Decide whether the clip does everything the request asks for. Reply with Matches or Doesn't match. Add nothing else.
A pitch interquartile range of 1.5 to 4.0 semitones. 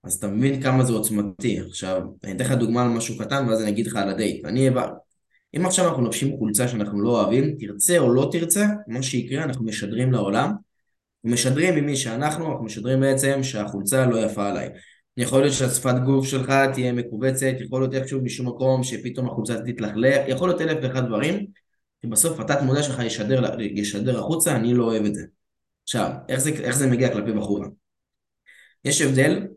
Matches